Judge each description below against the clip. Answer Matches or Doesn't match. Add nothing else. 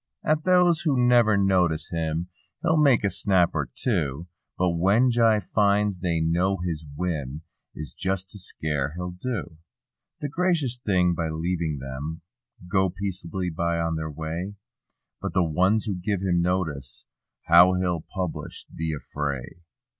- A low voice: Matches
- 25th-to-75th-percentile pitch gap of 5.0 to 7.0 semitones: Doesn't match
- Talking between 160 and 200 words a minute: Doesn't match